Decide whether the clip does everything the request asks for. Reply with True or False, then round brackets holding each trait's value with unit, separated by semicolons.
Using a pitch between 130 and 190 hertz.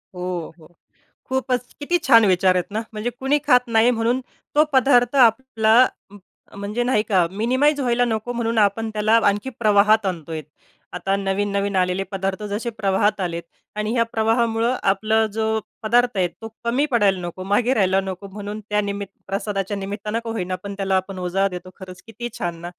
False (210 Hz)